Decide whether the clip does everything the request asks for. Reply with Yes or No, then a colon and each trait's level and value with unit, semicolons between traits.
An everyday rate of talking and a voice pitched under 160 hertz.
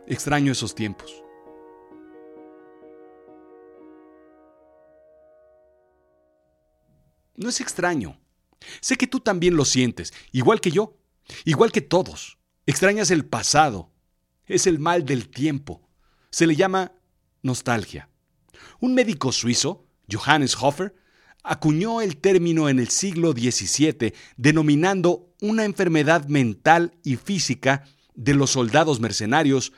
No: slow, 105 wpm; low, 135 Hz